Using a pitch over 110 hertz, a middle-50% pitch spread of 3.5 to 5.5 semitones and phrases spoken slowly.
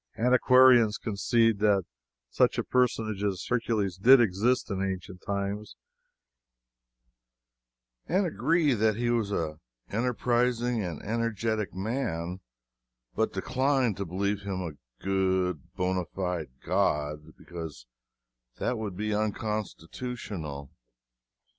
No: low, 105 Hz; average, 4.3 semitones; slow, 105 wpm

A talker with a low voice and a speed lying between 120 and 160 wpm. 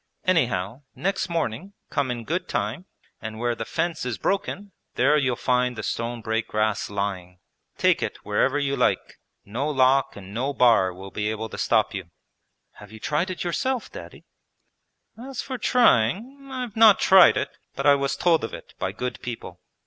No: low, 125 Hz; average, 180 wpm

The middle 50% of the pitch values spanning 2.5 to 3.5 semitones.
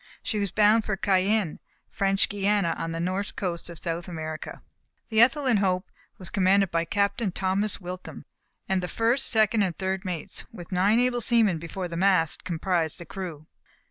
Yes: average, 3.1 semitones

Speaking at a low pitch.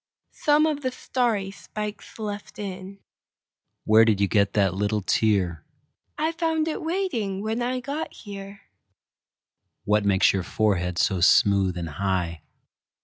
No: high, 190 Hz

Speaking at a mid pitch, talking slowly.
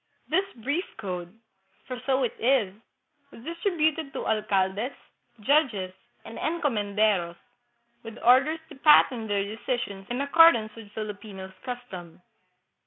No: high, 230 Hz; slow, 120 wpm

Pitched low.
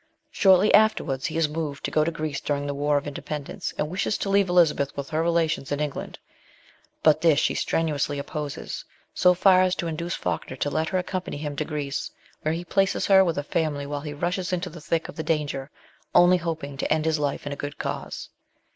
No: medium, 155 Hz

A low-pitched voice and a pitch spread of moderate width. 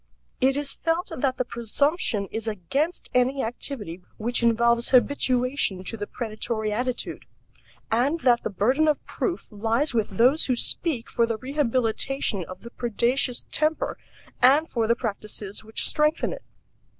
No: high, 240 Hz; average, 3.9 semitones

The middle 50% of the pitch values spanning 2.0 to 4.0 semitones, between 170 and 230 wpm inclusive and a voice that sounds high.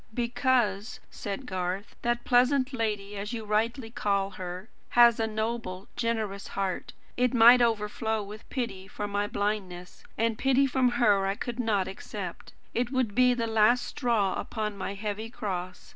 No: average, 3.3 semitones; average, 160 wpm; high, 220 Hz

